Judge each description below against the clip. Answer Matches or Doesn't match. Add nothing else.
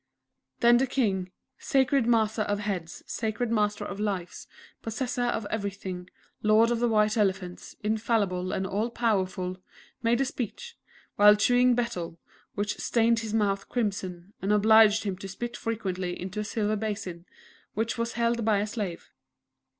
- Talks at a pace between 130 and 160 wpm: Matches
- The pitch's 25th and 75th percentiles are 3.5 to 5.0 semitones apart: Doesn't match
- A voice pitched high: Matches